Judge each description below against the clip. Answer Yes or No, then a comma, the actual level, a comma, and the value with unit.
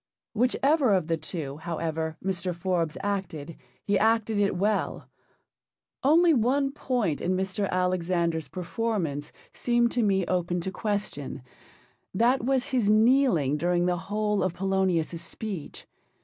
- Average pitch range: Yes, average, 4.8 semitones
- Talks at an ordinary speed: No, slow, 130 wpm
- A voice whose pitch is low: No, high, 190 Hz